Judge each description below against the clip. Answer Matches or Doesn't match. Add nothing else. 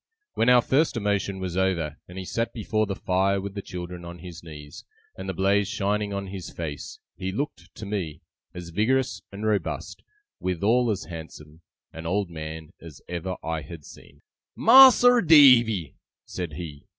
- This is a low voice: Matches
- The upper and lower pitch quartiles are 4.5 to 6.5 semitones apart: Doesn't match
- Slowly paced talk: Doesn't match